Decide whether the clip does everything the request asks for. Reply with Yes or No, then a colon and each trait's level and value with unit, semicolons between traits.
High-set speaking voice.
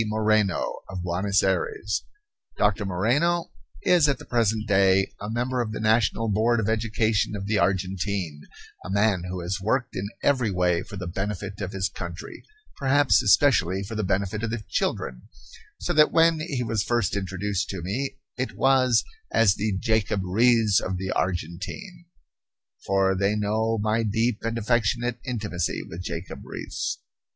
No: low, 105 Hz